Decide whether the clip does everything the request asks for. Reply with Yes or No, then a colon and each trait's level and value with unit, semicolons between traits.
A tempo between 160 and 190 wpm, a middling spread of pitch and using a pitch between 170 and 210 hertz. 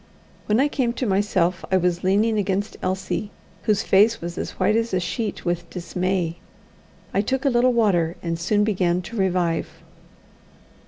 Yes: average, 165 wpm; average, 3.6 semitones; high, 190 Hz